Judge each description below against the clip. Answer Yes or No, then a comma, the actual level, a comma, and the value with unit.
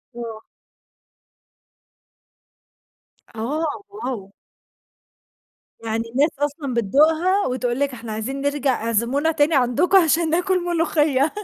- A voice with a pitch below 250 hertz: No, very high, 280 Hz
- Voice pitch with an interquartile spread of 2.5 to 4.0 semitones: No, average, 5.1 semitones